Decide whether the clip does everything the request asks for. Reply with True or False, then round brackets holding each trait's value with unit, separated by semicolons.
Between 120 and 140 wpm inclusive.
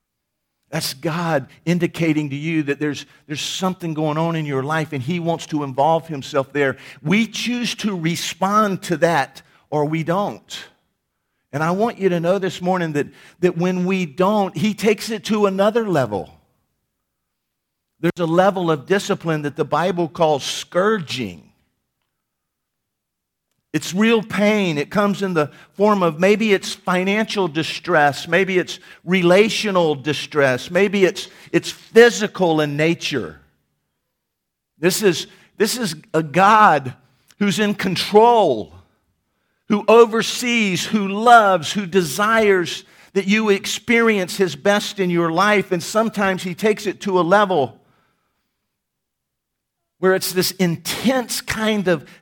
True (135 wpm)